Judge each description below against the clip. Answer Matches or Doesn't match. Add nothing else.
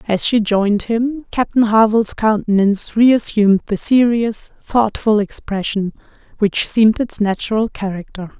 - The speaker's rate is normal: Doesn't match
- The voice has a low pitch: Doesn't match